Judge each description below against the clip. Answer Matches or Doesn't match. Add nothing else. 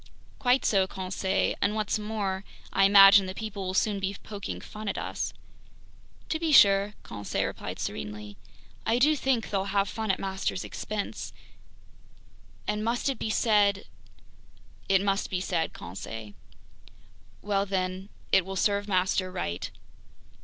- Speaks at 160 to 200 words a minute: Doesn't match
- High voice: Matches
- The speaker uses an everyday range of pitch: Doesn't match